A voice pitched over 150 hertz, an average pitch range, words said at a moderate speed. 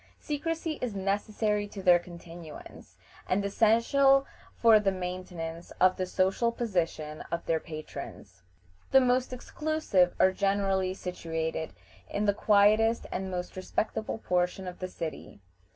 No: high, 190 Hz; average, 3.8 semitones; slow, 130 wpm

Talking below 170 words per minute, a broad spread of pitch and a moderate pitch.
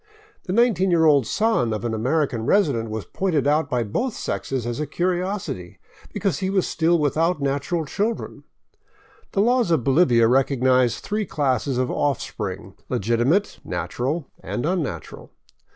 Yes: average, 150 wpm; wide, 6.6 semitones; medium, 145 Hz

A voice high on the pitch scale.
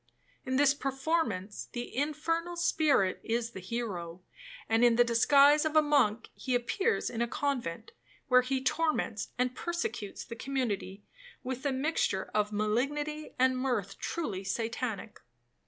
Yes: very high, 255 Hz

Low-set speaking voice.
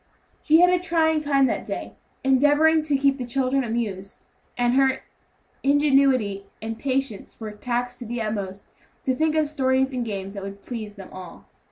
No: very high, 255 Hz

